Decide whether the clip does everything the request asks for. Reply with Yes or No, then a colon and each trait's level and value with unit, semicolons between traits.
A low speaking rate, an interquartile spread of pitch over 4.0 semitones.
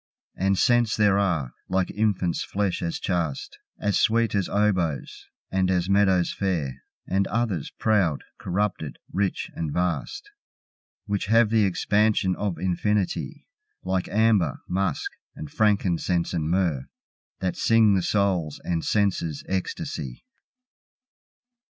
No: slow, 120 wpm; average, 3.1 semitones